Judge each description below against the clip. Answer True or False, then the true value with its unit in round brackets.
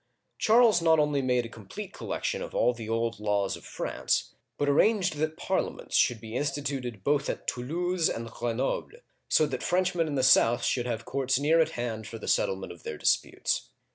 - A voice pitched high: False (135 Hz)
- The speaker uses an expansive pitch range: True (5.9 semitones)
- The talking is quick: False (195 wpm)